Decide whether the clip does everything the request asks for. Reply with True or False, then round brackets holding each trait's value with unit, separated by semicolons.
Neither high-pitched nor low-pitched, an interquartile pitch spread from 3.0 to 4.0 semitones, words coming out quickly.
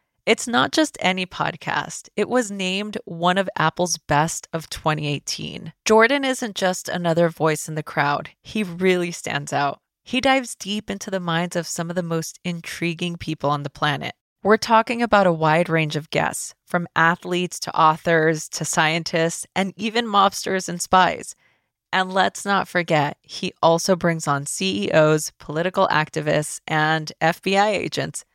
False (175 Hz; 3.7 semitones; 160 wpm)